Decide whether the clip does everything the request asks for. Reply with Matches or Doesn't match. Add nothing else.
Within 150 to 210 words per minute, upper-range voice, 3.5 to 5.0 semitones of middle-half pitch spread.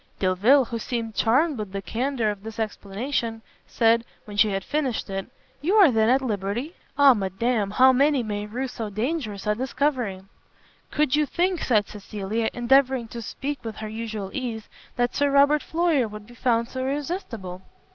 Matches